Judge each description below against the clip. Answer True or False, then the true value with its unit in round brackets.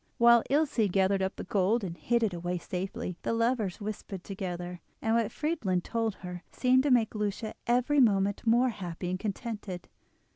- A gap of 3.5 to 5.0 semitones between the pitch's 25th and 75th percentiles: True (4.1 semitones)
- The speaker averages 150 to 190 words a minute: True (175 wpm)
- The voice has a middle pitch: False (210 Hz)